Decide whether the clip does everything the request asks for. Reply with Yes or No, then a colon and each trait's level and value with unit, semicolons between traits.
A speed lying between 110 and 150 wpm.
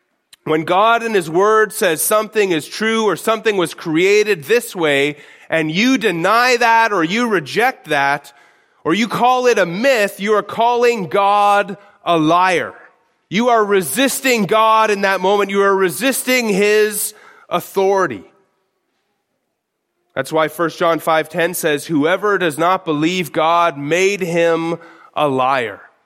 Yes: average, 145 wpm